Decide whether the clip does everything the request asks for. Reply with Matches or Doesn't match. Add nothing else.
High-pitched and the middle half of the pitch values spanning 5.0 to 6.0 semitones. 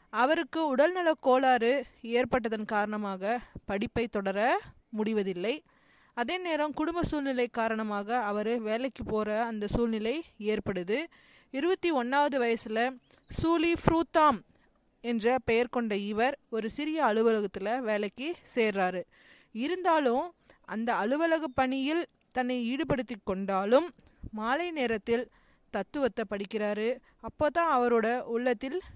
Doesn't match